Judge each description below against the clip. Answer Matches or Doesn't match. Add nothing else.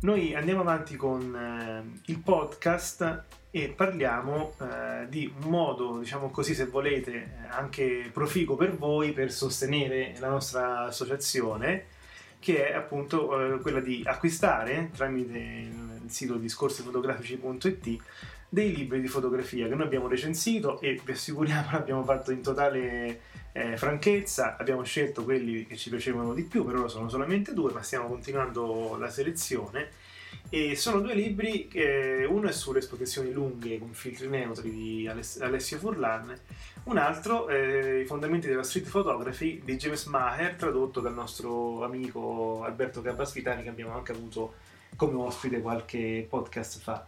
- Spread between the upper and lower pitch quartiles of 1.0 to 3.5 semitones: Doesn't match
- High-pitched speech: Doesn't match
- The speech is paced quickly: Doesn't match